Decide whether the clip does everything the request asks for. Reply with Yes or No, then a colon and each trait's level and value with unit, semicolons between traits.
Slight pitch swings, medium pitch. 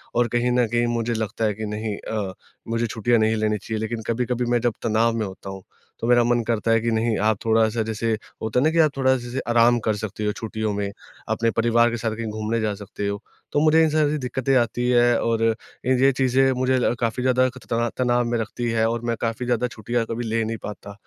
No: narrow, 1.8 semitones; low, 115 Hz